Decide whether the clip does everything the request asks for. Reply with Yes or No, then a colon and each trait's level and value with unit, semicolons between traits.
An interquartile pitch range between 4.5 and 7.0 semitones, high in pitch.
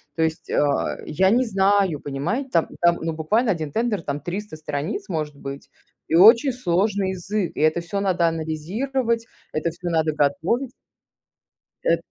No: average, 5.1 semitones; medium, 175 Hz